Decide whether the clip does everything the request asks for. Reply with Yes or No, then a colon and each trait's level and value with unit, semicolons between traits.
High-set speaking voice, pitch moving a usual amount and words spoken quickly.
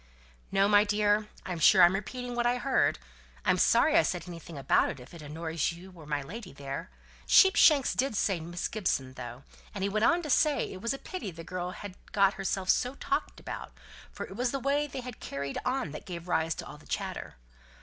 No: high, 195 Hz; wide, 6.8 semitones; fast, 220 wpm